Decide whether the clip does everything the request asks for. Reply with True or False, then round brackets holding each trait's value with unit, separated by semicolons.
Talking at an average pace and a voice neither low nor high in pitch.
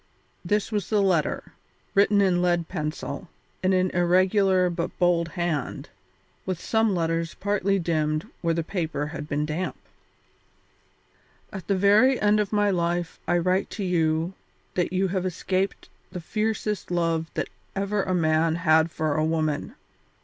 True (150 wpm; 175 Hz)